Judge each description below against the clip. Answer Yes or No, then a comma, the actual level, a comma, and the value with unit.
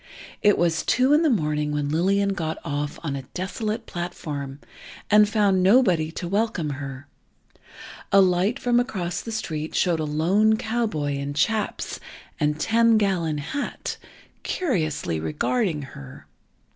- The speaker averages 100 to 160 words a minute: Yes, average, 140 wpm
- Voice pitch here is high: No, medium, 175 Hz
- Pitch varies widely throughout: Yes, wide, 6.4 semitones